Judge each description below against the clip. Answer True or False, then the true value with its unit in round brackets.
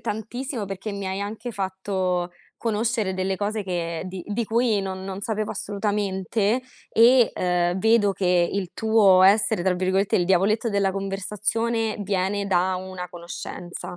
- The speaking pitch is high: True (195 Hz)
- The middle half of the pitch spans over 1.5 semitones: True (2.5 semitones)